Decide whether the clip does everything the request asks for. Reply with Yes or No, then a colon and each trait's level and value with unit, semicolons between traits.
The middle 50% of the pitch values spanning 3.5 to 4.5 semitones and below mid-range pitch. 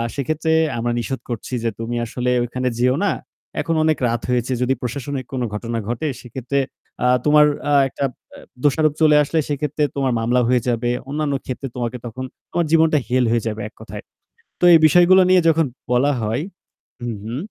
Yes: average, 4.0 semitones; low, 130 Hz